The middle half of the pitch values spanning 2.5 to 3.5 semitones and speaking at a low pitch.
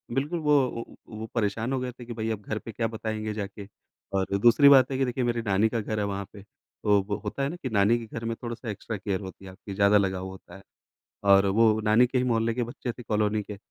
Yes: average, 2.9 semitones; low, 110 Hz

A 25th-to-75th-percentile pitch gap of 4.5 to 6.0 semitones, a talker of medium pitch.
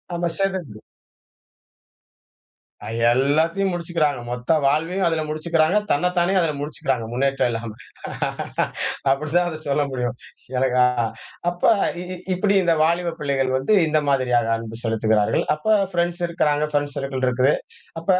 Yes: average, 4.9 semitones; medium, 150 Hz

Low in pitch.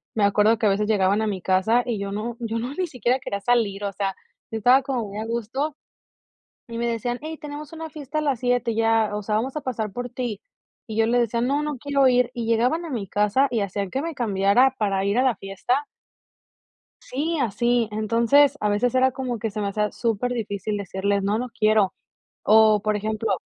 No: high, 230 Hz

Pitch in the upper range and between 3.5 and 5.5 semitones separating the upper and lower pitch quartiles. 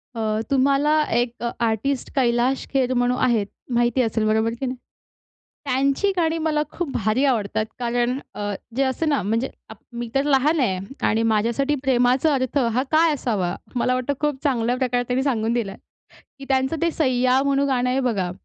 No: very high, 255 Hz; average, 2.9 semitones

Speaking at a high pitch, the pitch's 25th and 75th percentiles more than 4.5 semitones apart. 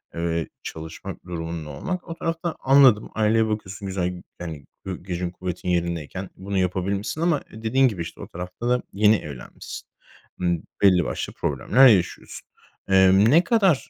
No: very low, 95 Hz; average, 5.1 semitones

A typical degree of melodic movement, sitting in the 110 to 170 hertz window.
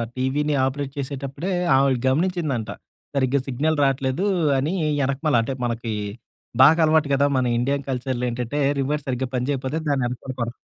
No: narrow, 2.3 semitones; low, 135 Hz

